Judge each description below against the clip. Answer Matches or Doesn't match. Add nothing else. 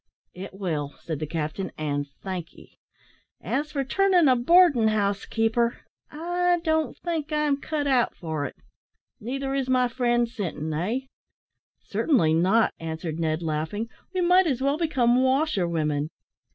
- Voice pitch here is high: Matches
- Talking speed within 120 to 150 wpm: Matches